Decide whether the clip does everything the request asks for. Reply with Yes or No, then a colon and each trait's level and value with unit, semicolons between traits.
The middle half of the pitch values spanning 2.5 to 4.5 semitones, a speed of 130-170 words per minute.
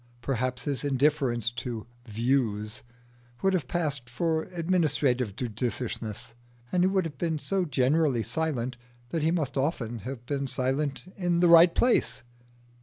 No: average, 5.2 semitones; average, 140 wpm